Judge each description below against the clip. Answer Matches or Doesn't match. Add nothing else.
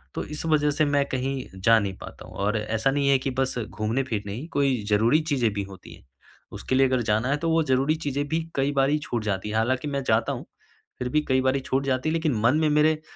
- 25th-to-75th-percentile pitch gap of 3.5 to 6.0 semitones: Matches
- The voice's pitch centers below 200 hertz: Matches